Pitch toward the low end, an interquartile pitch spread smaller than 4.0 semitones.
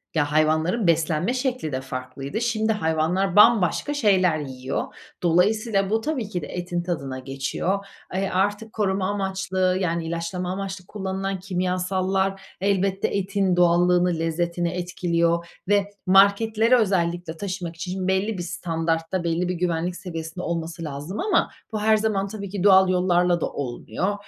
No: medium, 185 Hz; average, 2.9 semitones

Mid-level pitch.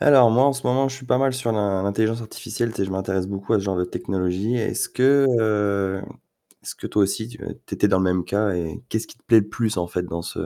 No: low, 105 Hz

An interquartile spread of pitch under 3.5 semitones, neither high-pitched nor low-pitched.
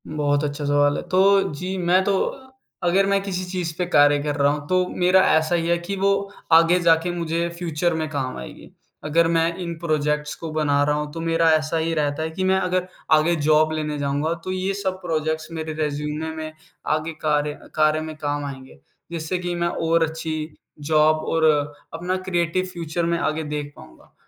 Yes: narrow, 2.6 semitones; medium, 160 Hz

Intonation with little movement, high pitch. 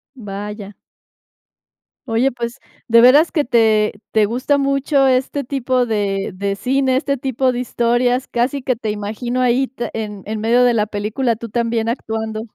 No: average, 3.0 semitones; high, 235 Hz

